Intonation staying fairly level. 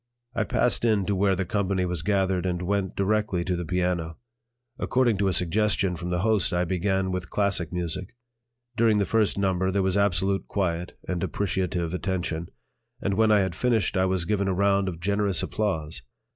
Yes: narrow, 2.3 semitones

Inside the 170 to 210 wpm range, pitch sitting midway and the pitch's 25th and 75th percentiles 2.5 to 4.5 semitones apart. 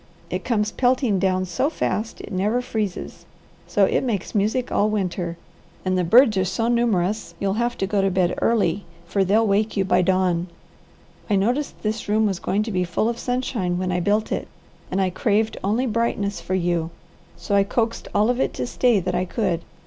No: average, 200 wpm; high, 205 Hz; average, 3.5 semitones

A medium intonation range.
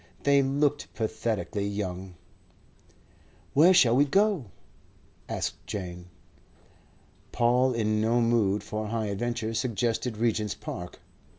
Yes: average, 3.1 semitones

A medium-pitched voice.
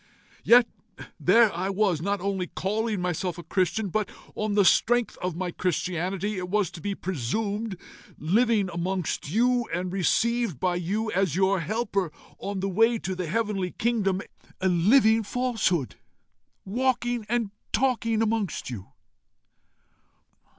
No: high, 195 Hz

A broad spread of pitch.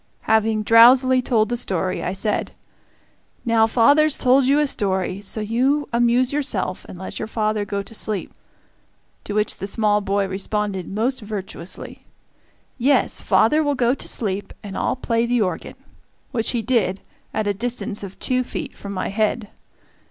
No: average, 3.6 semitones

